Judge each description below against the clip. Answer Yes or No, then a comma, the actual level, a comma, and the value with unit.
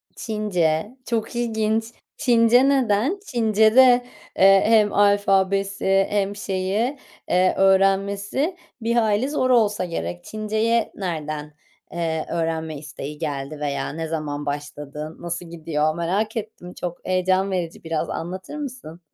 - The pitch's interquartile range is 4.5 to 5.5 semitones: Yes, average, 5.1 semitones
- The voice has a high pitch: Yes, high, 195 Hz